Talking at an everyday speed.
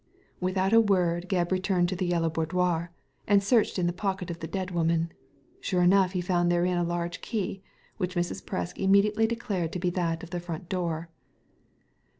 Yes: average, 185 wpm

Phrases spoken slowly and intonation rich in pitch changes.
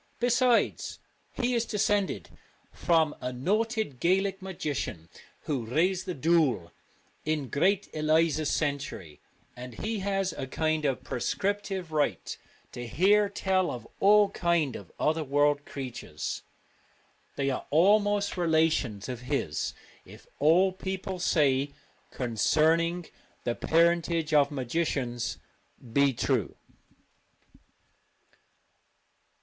Yes: slow, 110 wpm; wide, 5.9 semitones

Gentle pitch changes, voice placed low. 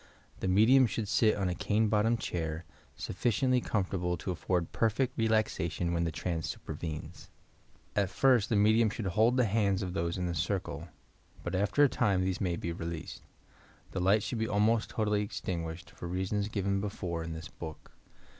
No: average, 4.0 semitones; low, 100 Hz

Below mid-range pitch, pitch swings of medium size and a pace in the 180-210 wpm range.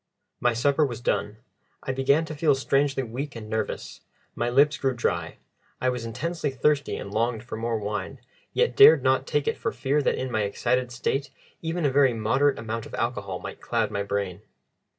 Yes: low, 130 Hz; average, 4.2 semitones; average, 190 wpm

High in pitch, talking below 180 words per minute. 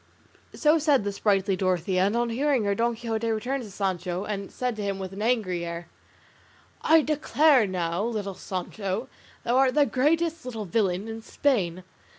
Yes: high, 215 Hz; average, 170 wpm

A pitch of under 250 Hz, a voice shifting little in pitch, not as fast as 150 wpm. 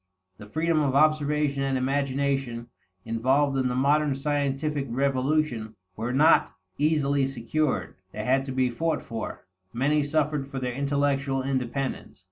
Yes: low, 135 Hz; narrow, 2.3 semitones; slow, 135 wpm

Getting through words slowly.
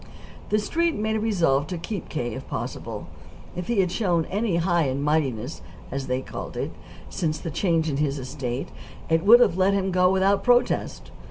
No: average, 190 wpm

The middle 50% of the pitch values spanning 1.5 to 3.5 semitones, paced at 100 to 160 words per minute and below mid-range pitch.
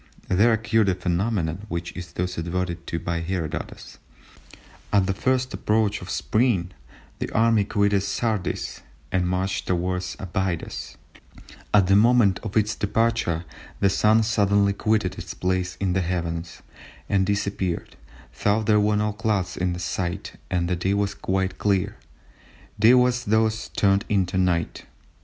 Yes: average, 2.8 semitones; average, 145 wpm; very low, 95 Hz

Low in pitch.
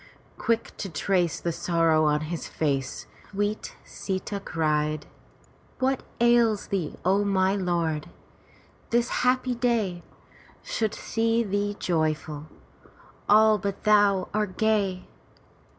No: high, 195 Hz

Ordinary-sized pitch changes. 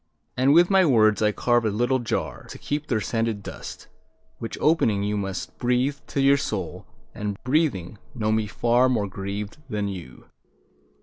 Yes: average, 4.0 semitones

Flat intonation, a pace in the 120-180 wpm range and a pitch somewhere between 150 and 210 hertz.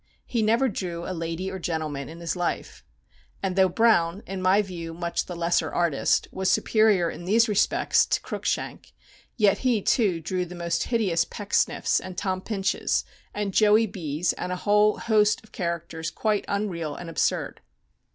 No: average, 3.6 semitones; average, 170 wpm; medium, 185 Hz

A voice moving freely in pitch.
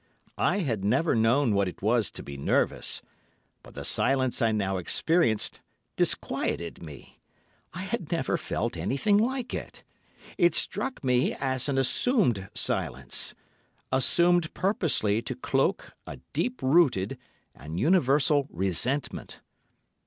Yes: wide, 8.6 semitones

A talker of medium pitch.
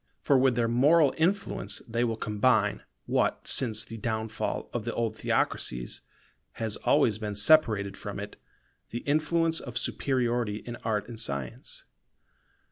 No: low, 115 Hz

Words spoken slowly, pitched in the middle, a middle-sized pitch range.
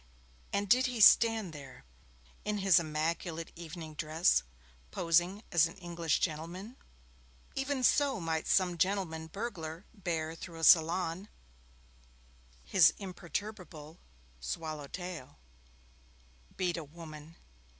Yes: slow, 110 wpm; medium, 170 Hz; average, 3.5 semitones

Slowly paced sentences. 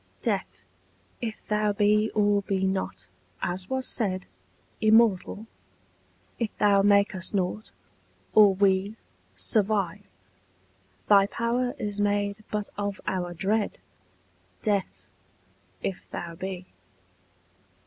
Yes: slow, 105 wpm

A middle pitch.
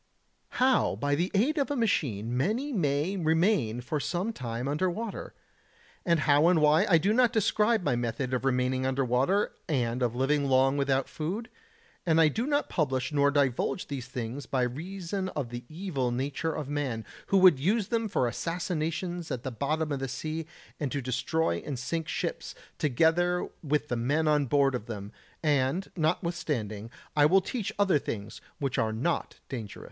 Yes: medium, 150 Hz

